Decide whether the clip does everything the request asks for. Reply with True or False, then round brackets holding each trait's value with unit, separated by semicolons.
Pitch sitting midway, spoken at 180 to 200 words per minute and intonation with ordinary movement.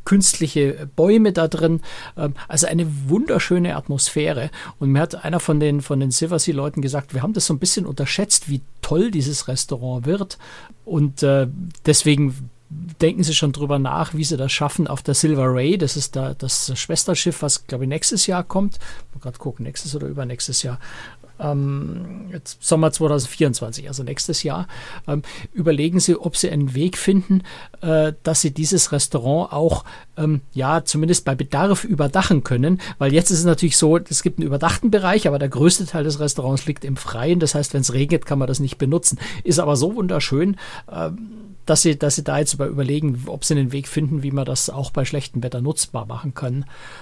True (150 Hz; 185 wpm; 3.6 semitones)